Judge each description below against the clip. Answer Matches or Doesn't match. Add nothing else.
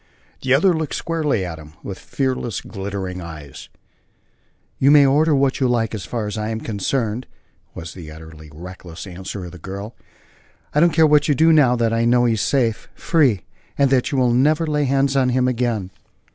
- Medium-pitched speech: Doesn't match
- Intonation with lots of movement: Matches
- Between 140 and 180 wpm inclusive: Doesn't match